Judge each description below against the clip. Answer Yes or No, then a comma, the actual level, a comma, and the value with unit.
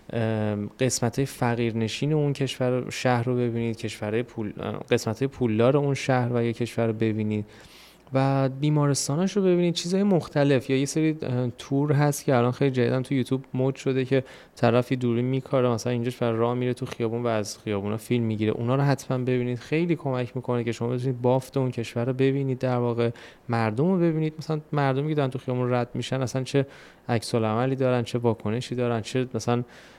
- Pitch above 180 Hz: No, low, 125 Hz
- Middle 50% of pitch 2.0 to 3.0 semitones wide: Yes, narrow, 2.4 semitones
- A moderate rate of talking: No, fast, 185 wpm